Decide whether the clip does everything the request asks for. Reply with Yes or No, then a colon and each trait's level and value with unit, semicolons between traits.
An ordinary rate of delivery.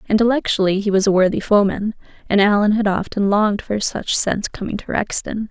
Yes: average, 185 wpm